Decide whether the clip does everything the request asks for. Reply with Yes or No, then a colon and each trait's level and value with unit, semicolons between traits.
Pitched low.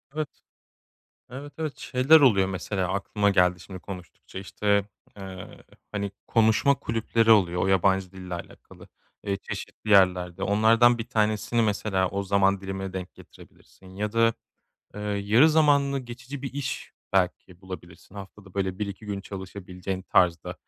Yes: low, 100 Hz